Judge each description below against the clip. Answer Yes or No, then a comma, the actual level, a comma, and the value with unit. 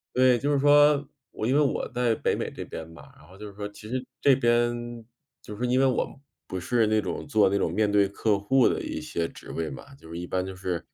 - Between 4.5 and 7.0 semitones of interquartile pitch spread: Yes, average, 4.8 semitones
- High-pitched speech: No, low, 110 Hz